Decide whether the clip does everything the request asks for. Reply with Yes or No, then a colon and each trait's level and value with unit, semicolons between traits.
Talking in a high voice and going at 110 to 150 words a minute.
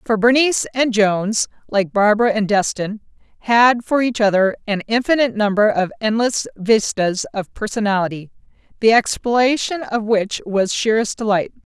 Yes: high, 215 Hz; average, 140 wpm